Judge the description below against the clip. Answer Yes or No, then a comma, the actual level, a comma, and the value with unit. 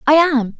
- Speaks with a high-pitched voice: Yes, very high, 285 Hz